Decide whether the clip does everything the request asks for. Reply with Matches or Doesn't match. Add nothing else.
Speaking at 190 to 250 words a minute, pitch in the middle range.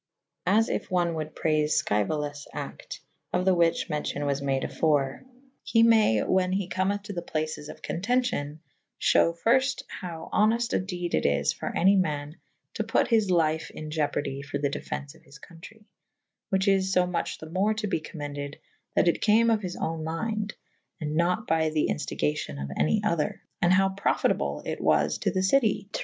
Matches